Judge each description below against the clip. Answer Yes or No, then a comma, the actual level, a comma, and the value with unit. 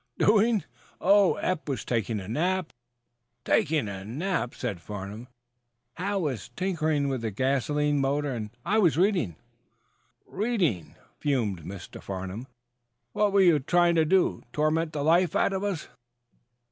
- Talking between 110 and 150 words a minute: Yes, slow, 135 wpm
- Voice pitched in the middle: Yes, medium, 145 Hz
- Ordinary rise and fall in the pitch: No, wide, 7.3 semitones